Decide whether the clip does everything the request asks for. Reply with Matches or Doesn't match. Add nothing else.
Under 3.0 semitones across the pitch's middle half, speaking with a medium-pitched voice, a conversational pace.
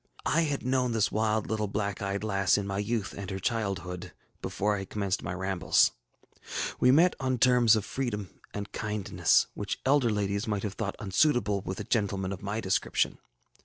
Doesn't match